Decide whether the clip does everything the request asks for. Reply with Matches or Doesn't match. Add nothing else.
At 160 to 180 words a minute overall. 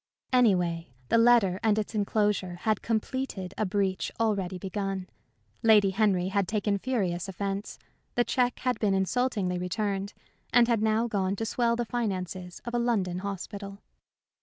Doesn't match